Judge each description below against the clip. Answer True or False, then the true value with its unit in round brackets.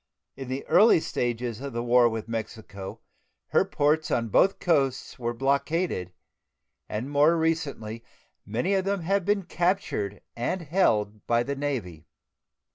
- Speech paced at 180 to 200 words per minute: False (140 wpm)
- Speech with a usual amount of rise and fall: False (6.4 semitones)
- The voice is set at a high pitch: False (135 Hz)